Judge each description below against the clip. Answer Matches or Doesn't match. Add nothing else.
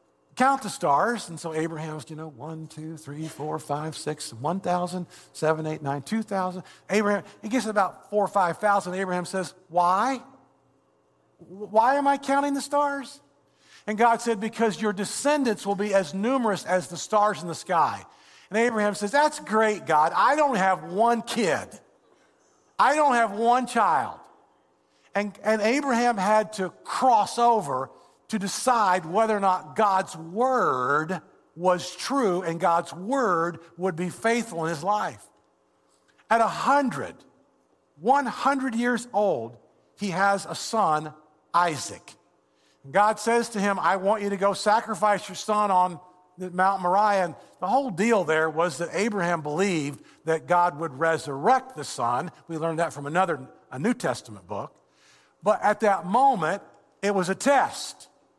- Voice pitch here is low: Doesn't match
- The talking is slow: Doesn't match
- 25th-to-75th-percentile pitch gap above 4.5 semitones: Matches